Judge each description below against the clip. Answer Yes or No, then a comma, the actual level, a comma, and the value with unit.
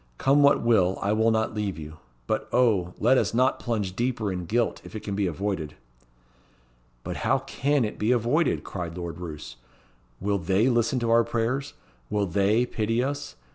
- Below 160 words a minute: No, average, 180 wpm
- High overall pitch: No, low, 110 Hz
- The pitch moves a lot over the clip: No, average, 4.4 semitones